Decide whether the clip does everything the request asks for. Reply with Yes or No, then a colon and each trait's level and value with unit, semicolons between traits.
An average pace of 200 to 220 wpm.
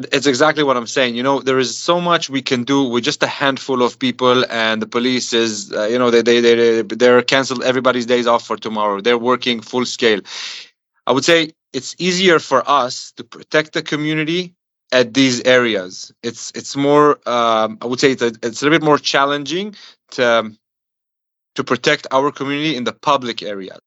Yes: fast, 205 wpm